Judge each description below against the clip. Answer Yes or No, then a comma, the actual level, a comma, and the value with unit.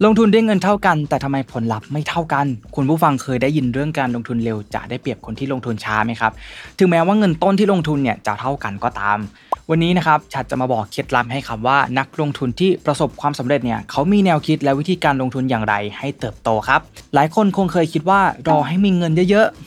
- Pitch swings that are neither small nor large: No, wide, 5.7 semitones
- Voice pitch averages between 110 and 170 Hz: Yes, medium, 140 Hz